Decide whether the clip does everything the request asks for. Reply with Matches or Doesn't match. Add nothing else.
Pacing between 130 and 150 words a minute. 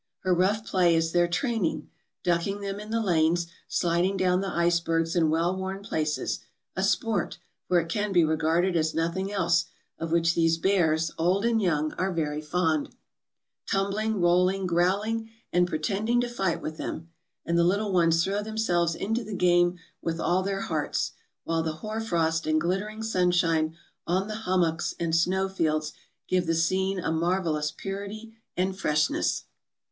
Doesn't match